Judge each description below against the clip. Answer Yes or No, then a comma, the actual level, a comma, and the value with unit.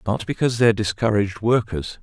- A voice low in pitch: Yes, low, 105 Hz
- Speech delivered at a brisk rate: No, average, 180 wpm